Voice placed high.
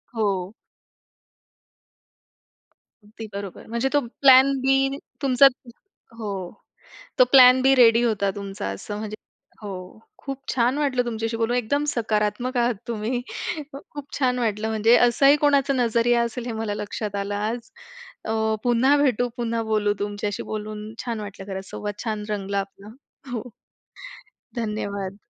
Yes: high, 225 Hz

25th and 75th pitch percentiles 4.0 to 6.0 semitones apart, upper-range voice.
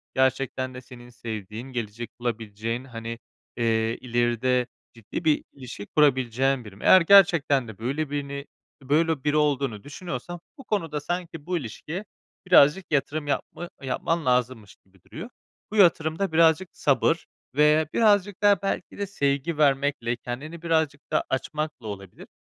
No: average, 5.1 semitones; medium, 140 Hz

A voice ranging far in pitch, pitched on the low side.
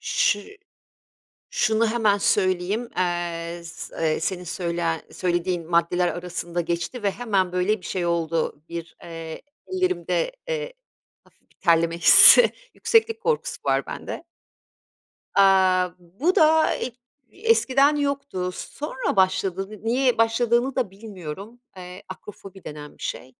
No: wide, 6.0 semitones; high, 190 Hz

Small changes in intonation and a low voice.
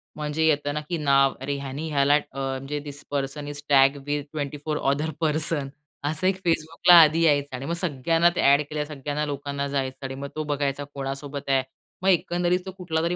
No: narrow, 2.3 semitones; medium, 145 Hz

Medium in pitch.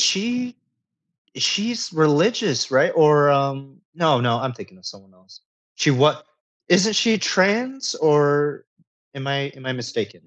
Yes: medium, 150 Hz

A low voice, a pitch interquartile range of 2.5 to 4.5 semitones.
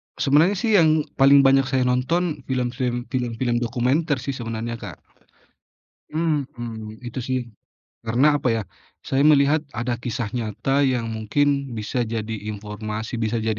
Yes: low, 125 Hz; average, 3.6 semitones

